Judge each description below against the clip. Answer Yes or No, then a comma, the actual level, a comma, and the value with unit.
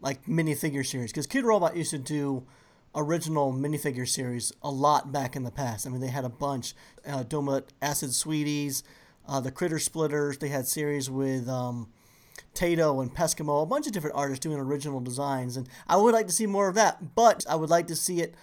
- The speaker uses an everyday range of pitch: Yes, average, 3.1 semitones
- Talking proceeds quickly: Yes, fast, 210 wpm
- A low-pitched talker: No, medium, 145 Hz